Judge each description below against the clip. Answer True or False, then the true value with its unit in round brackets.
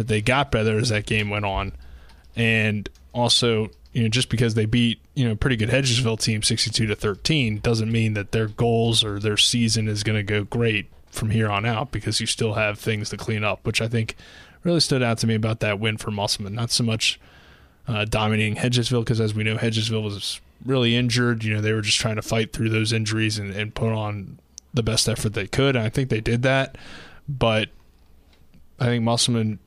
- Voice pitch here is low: True (110 Hz)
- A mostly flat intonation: True (1.9 semitones)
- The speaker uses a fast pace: True (220 wpm)